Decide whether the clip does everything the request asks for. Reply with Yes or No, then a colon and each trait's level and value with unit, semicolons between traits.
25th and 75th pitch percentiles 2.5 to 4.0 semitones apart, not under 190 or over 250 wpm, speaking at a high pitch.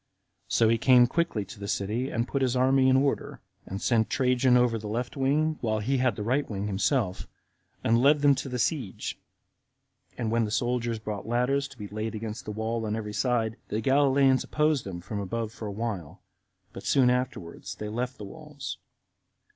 No: average, 3.5 semitones; average, 195 wpm; low, 120 Hz